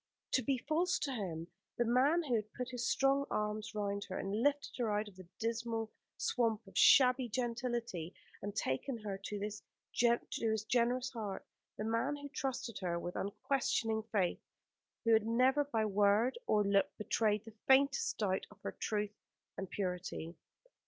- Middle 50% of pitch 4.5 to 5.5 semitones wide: No, average, 3.6 semitones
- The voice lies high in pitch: Yes, high, 225 Hz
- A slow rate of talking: No, average, 165 wpm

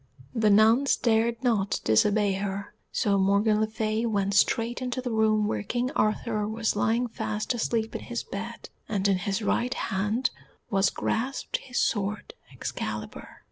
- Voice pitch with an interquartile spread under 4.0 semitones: Yes, narrow, 2.5 semitones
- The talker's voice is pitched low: No, high, 215 Hz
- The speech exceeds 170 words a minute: No, average, 155 wpm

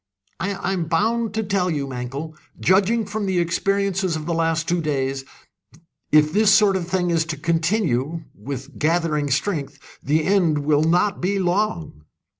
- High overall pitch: No, medium, 170 Hz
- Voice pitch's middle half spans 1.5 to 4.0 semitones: No, average, 4.4 semitones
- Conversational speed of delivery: Yes, average, 160 wpm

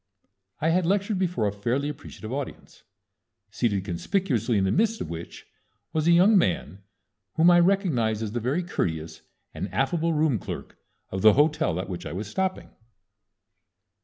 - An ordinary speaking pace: Yes, average, 160 wpm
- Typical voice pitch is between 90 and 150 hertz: Yes, low, 135 Hz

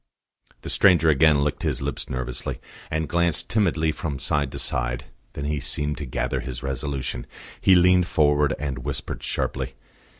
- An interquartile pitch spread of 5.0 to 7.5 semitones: No, average, 3.0 semitones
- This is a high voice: No, very low, 75 Hz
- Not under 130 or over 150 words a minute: No, average, 160 wpm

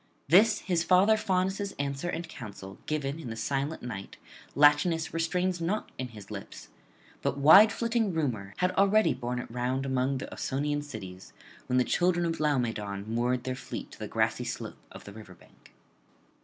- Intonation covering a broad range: Yes, wide, 6.5 semitones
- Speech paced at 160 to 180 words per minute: Yes, average, 170 wpm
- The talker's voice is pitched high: No, medium, 140 Hz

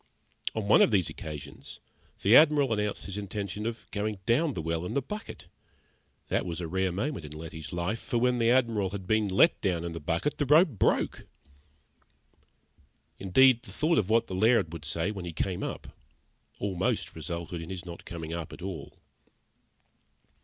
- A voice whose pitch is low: Yes, low, 100 Hz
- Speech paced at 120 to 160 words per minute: No, average, 180 wpm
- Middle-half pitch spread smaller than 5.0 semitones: No, average, 5.3 semitones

